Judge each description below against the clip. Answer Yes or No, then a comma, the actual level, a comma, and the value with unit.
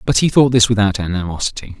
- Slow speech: No, average, 200 wpm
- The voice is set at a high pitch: No, low, 105 Hz